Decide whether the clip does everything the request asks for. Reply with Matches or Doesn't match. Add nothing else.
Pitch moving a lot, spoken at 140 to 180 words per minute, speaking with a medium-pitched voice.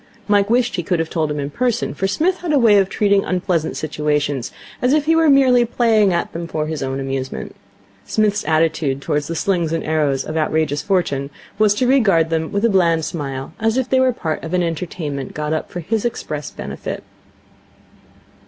Doesn't match